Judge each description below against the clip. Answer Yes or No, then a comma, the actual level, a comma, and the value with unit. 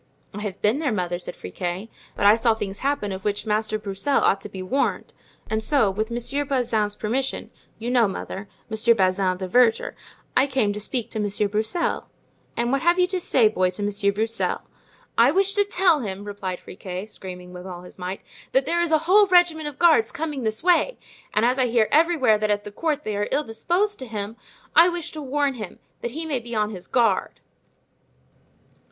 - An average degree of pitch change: No, wide, 5.9 semitones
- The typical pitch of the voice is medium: No, high, 225 Hz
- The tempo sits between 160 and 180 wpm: No, fast, 205 wpm